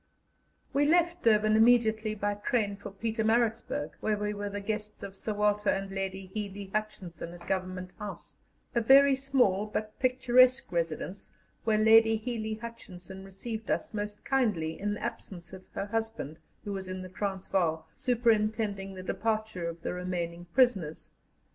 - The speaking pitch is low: No, high, 210 Hz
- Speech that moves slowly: No, average, 155 wpm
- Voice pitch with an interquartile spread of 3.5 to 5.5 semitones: No, average, 2.9 semitones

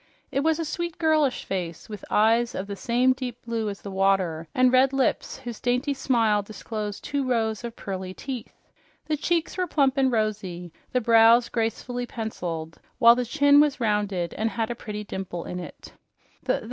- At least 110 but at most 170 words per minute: No, average, 180 wpm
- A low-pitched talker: No, high, 230 Hz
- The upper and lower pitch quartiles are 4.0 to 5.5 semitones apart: Yes, average, 4.3 semitones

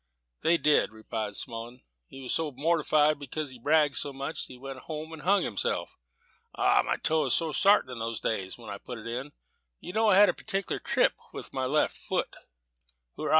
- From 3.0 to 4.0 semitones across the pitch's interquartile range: No, average, 4.6 semitones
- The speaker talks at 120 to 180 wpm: No, fast, 205 wpm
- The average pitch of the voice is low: No, medium, 145 Hz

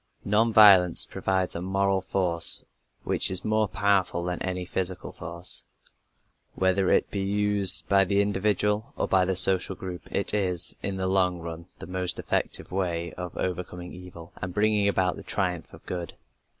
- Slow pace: No, average, 165 wpm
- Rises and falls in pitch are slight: Yes, narrow, 1.8 semitones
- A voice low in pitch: Yes, very low, 95 Hz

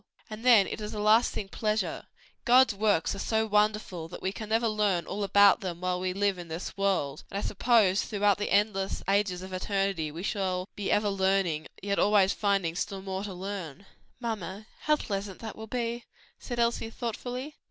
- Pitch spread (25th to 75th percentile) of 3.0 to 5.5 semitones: No, narrow, 2.4 semitones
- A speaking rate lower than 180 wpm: No, average, 190 wpm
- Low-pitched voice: No, high, 200 Hz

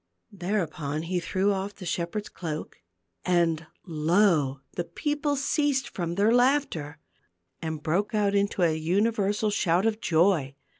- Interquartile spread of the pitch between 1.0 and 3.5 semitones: No, average, 4.4 semitones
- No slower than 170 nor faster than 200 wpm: No, slow, 135 wpm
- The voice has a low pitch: No, medium, 185 Hz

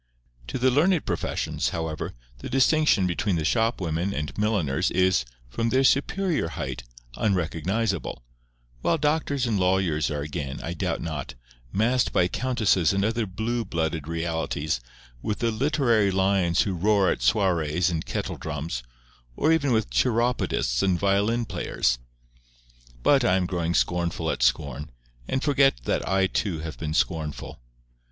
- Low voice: Yes, very low, 95 Hz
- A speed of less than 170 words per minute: Yes, average, 145 wpm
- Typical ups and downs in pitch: No, wide, 6.3 semitones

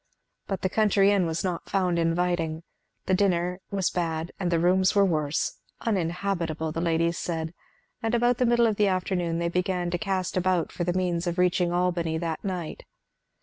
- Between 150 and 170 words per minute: No, average, 185 wpm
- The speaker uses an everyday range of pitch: No, narrow, 2.1 semitones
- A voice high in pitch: No, medium, 180 Hz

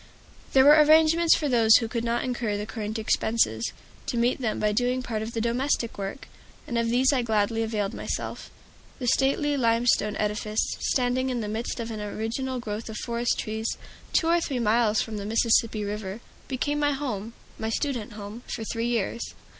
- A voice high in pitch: Yes, high, 230 Hz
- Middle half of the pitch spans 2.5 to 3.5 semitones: Yes, average, 2.8 semitones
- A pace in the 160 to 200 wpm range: Yes, average, 185 wpm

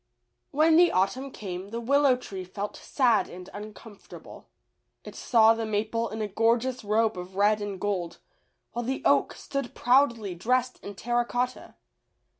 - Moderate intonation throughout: Yes, average, 3.6 semitones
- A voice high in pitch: Yes, high, 225 Hz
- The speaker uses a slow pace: No, average, 155 wpm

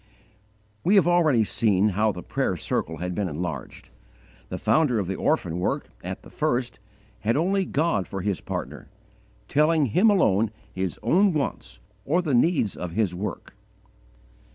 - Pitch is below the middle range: Yes, low, 110 Hz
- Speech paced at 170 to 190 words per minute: No, average, 155 wpm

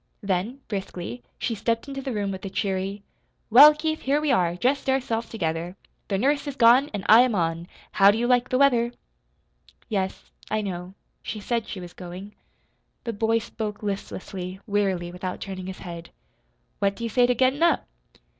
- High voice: Yes, high, 210 Hz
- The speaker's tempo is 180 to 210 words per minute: Yes, average, 185 wpm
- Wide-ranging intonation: No, average, 4.7 semitones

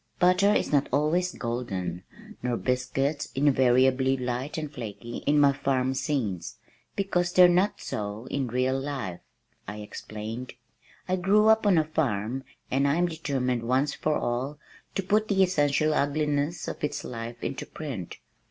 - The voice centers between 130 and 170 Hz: Yes, medium, 140 Hz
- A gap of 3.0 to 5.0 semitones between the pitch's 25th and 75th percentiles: Yes, average, 4.1 semitones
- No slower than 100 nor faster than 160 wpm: Yes, average, 150 wpm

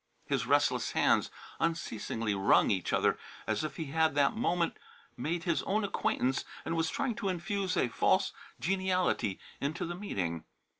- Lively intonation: Yes, wide, 6.0 semitones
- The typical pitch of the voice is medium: Yes, medium, 165 Hz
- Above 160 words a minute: No, average, 155 wpm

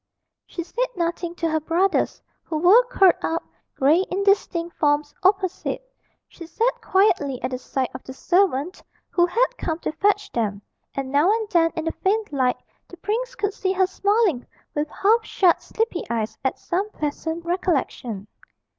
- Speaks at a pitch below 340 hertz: No, very high, 345 Hz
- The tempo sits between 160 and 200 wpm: Yes, average, 165 wpm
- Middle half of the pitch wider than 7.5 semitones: No, average, 5.2 semitones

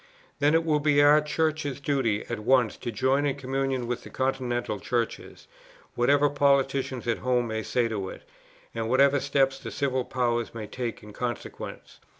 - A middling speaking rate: Yes, average, 170 wpm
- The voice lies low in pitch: Yes, low, 130 Hz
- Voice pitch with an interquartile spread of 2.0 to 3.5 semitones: Yes, average, 2.9 semitones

